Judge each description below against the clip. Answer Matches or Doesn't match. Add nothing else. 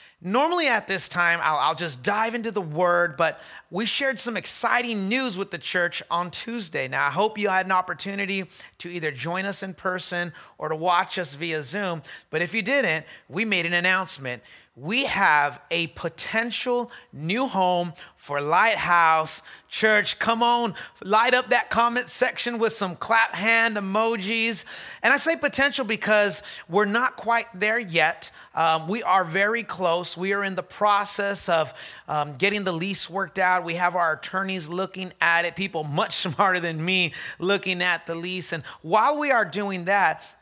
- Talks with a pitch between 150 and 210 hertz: Matches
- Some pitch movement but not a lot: Matches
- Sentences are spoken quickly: Doesn't match